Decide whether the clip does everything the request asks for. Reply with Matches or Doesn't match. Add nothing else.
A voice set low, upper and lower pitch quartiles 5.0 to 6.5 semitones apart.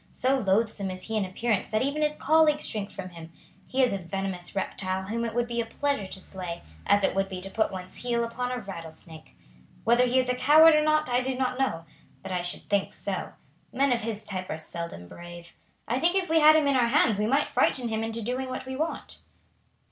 Doesn't match